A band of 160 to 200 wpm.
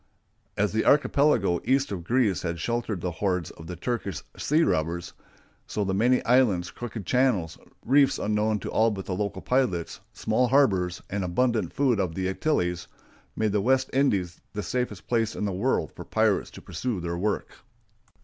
Yes: average, 175 wpm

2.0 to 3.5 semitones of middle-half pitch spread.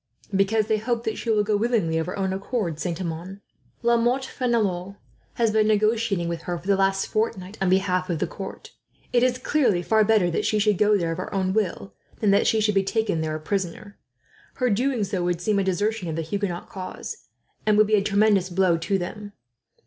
Yes: average, 3.2 semitones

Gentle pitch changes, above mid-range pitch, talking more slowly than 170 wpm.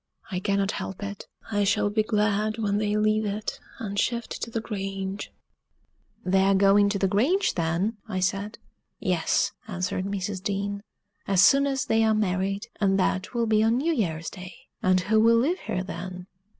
No: narrow, 2.2 semitones; high, 200 Hz; average, 180 wpm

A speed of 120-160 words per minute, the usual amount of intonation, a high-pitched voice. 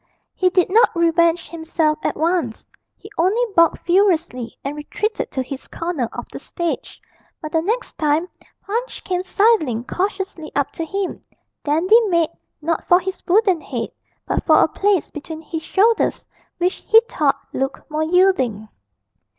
Yes: average, 155 wpm; average, 3.9 semitones; very high, 340 Hz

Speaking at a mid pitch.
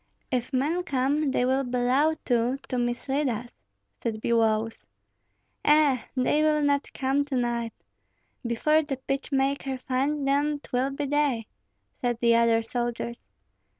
No: very high, 260 Hz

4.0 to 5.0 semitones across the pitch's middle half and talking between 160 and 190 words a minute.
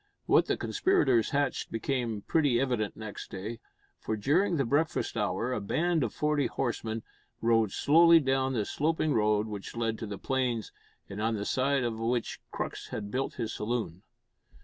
Yes: average, 4.3 semitones; average, 170 wpm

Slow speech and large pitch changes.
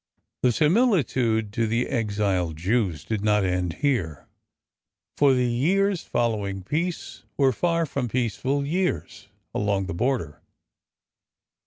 Yes: slow, 120 wpm; wide, 5.7 semitones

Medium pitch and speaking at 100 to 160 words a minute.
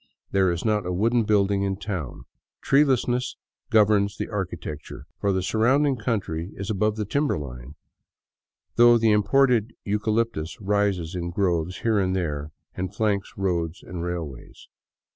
No: low, 100 Hz; average, 145 wpm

